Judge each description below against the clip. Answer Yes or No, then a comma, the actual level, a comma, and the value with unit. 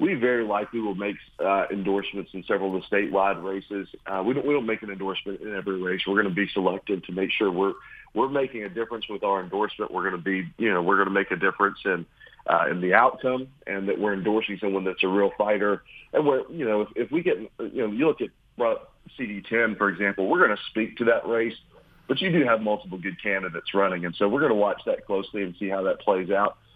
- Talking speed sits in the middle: No, fast, 250 wpm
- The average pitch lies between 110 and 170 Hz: No, low, 100 Hz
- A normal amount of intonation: No, narrow, 2.0 semitones